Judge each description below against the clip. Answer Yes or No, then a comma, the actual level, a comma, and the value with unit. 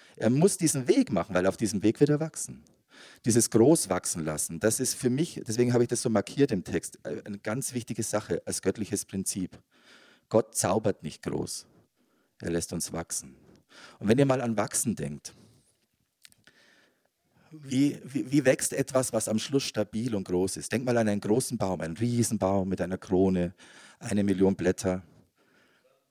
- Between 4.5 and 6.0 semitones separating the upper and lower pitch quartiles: Yes, average, 5.1 semitones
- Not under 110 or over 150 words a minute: No, average, 175 wpm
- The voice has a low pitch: Yes, low, 110 Hz